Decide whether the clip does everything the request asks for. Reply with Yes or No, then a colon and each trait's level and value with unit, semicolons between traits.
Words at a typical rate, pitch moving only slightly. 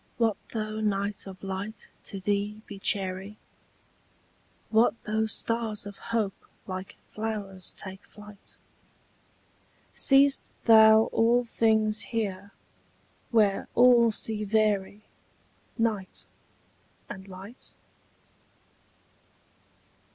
No: slow, 90 wpm; narrow, 2.2 semitones